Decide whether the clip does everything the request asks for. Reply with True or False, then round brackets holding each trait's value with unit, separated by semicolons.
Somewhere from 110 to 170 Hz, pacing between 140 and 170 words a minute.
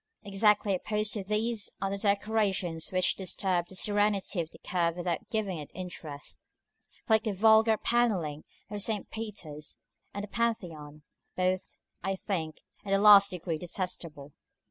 False (195 Hz; 145 wpm)